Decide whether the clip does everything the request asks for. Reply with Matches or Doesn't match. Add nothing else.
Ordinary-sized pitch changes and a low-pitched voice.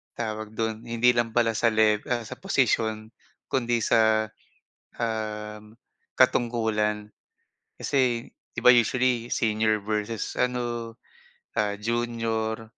Doesn't match